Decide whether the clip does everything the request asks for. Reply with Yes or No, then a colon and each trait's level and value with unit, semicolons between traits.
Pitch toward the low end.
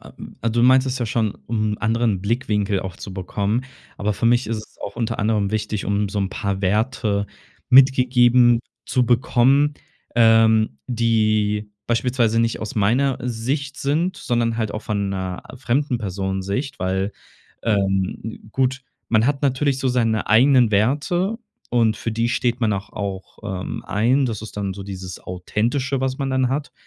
Yes: low, 115 Hz